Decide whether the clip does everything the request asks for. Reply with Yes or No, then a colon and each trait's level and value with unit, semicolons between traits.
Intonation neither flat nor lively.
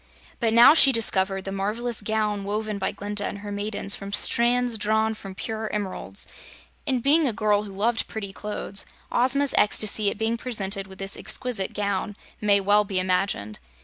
No: narrow, 2.3 semitones